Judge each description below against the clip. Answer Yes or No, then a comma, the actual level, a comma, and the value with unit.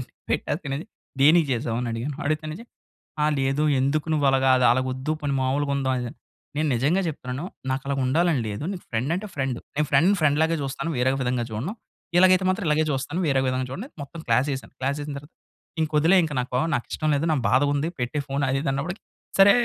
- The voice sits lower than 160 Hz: Yes, medium, 140 Hz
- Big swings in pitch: No, average, 3.2 semitones